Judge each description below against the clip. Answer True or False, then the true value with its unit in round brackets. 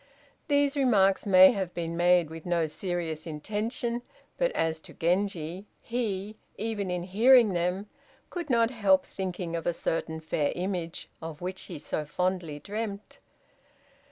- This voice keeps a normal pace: True (145 wpm)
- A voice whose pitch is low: False (185 Hz)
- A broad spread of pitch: False (4.2 semitones)